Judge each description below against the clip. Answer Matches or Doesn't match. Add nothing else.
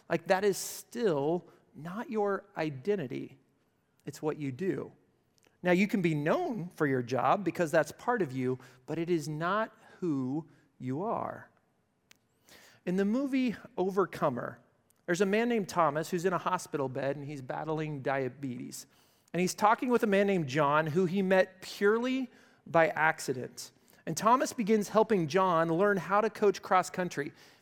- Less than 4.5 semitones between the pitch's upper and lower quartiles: Doesn't match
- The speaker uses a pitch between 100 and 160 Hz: Doesn't match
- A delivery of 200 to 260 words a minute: Doesn't match